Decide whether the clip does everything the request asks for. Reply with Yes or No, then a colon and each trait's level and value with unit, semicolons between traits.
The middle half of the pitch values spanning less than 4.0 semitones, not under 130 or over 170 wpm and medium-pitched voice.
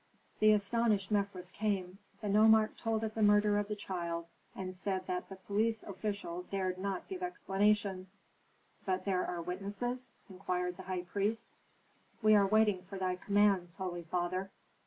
No: narrow, 2.4 semitones; average, 155 wpm; high, 195 Hz